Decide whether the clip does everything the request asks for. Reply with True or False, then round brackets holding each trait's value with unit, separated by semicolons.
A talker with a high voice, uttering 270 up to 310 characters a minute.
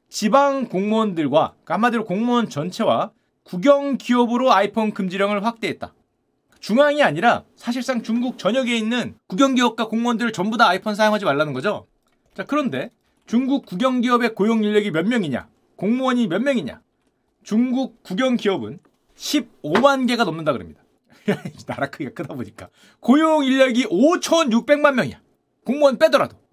False (240 Hz; 330 characters per minute)